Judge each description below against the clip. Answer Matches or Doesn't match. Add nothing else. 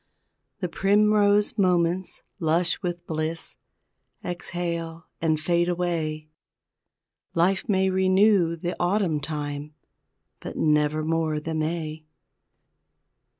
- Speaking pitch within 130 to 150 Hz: Doesn't match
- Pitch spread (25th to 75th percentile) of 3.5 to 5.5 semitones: Doesn't match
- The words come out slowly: Matches